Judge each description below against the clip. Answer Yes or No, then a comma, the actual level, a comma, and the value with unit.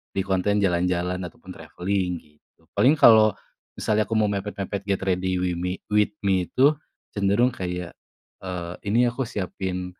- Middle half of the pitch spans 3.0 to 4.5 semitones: No, narrow, 2.5 semitones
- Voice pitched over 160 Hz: No, very low, 95 Hz